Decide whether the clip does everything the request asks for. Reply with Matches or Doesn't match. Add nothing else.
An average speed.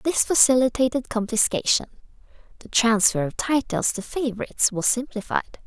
Doesn't match